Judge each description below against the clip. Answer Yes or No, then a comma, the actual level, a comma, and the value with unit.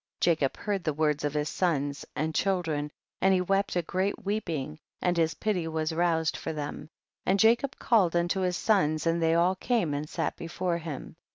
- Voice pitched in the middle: Yes, medium, 170 Hz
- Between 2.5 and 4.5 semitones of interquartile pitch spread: Yes, average, 3.5 semitones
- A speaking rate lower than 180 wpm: No, average, 195 wpm